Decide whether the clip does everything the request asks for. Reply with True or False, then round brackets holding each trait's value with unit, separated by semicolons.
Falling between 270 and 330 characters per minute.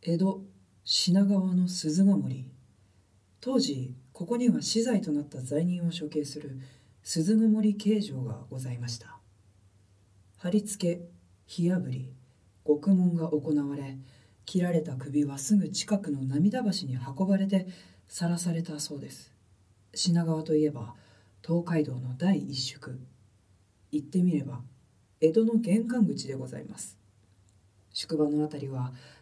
False (240 characters per minute)